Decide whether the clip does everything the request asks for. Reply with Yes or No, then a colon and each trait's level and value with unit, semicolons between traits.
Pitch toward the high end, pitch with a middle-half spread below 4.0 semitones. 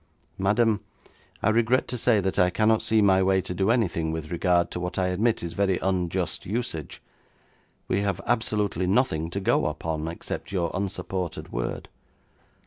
No: very low, 95 Hz; average, 3.5 semitones